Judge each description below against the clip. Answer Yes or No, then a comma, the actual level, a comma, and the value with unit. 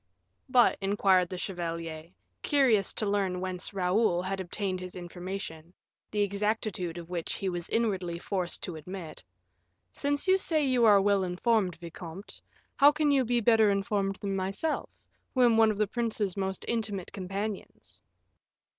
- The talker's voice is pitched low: No, high, 195 Hz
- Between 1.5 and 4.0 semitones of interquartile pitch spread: Yes, average, 3.4 semitones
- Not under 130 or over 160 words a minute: Yes, average, 155 wpm